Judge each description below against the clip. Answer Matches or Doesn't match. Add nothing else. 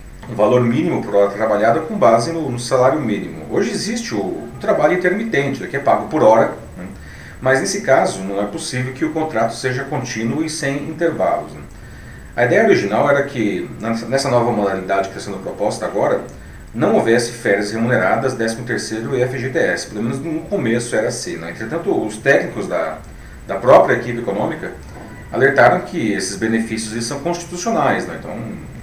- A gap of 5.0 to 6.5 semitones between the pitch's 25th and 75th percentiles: Doesn't match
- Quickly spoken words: Doesn't match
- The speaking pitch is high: Doesn't match